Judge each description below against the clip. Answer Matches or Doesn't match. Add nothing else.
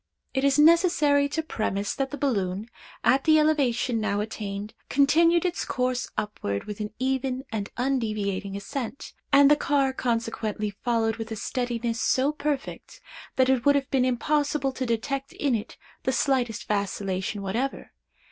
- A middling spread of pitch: Matches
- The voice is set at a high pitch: Matches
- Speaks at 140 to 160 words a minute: Matches